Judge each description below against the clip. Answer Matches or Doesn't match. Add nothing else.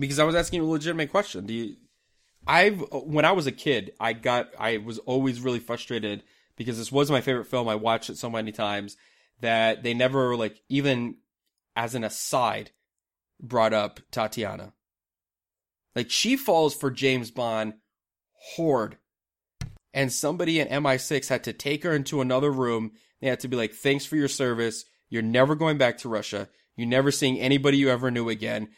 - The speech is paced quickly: Doesn't match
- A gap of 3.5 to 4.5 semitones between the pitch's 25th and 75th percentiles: Matches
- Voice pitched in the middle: Doesn't match